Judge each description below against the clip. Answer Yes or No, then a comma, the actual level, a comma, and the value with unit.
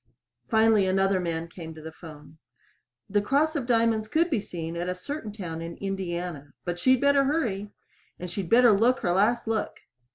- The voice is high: Yes, high, 195 Hz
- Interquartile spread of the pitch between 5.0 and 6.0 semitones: Yes, average, 5.3 semitones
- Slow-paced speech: No, average, 185 wpm